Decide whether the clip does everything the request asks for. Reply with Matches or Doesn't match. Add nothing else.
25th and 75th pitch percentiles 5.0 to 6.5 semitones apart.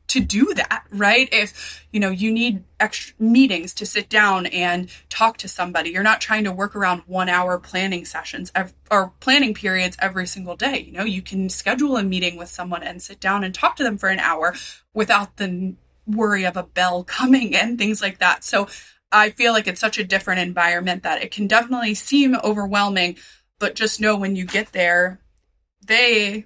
Doesn't match